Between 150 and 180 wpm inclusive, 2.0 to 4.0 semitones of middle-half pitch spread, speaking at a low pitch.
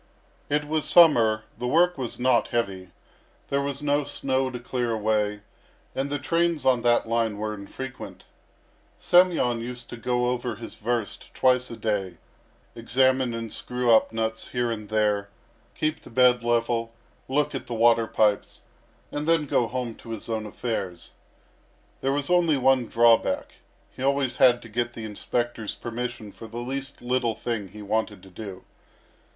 Yes: average, 165 wpm; average, 2.9 semitones; low, 120 Hz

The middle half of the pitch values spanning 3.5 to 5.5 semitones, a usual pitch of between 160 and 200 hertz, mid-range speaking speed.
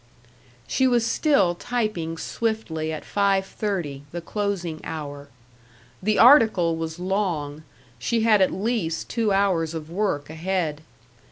No: average, 5.0 semitones; medium, 185 Hz; slow, 125 wpm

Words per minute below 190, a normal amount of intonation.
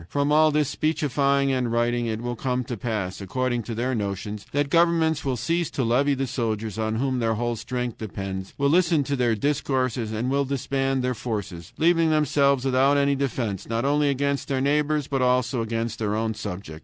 No: average, 195 wpm; average, 3.8 semitones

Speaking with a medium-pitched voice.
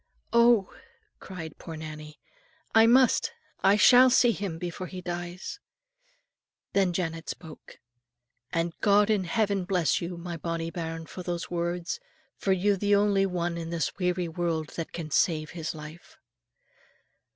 Yes: medium, 175 Hz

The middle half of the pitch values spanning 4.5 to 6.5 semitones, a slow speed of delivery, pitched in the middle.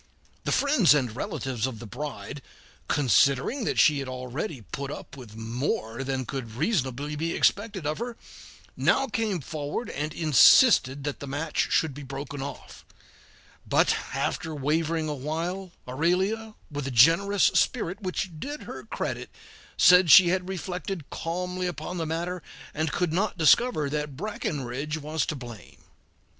No: average, 4.9 semitones; average, 150 wpm; medium, 155 Hz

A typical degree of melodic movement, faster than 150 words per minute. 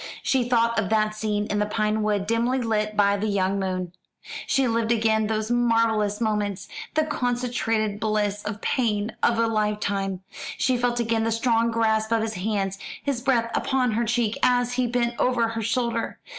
No: narrow, 2.2 semitones; average, 180 wpm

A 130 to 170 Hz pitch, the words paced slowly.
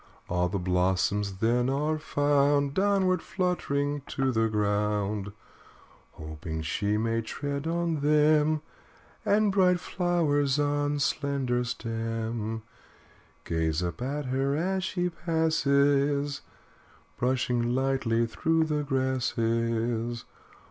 Yes: low, 135 Hz; slow, 100 wpm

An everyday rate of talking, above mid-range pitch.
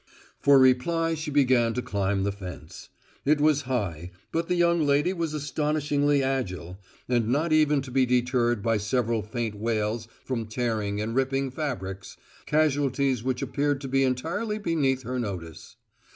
No: average, 155 wpm; low, 130 Hz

